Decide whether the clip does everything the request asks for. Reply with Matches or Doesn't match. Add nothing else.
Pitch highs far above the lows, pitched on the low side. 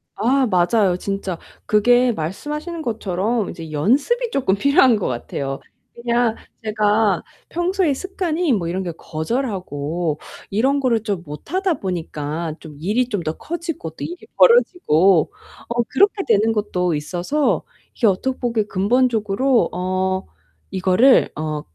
Doesn't match